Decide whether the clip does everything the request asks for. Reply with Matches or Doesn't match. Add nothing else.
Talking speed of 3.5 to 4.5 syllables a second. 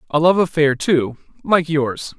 Matches